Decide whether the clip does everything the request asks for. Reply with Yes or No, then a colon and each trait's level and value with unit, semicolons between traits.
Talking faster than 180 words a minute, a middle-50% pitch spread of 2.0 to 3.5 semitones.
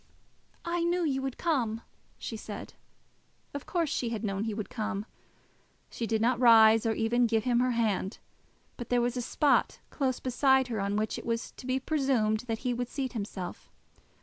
Yes: average, 195 wpm; average, 3.1 semitones